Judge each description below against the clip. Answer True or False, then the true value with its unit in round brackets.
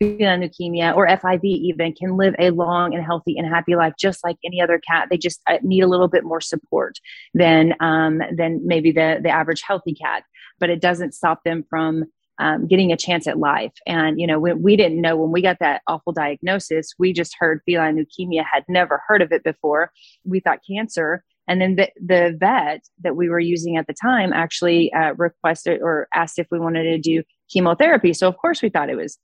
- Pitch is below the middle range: False (170 Hz)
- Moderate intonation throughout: False (1.8 semitones)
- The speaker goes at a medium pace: False (215 wpm)